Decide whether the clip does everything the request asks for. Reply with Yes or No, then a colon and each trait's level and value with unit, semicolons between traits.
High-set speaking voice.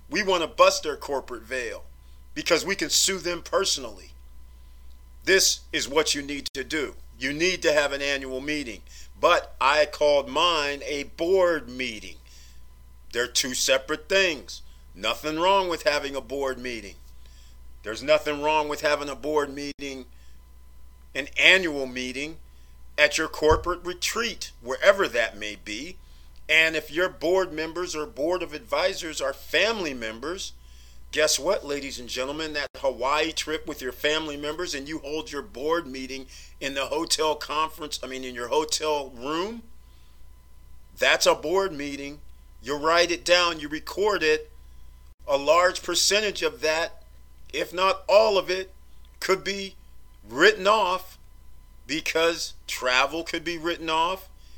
No: medium, 145 Hz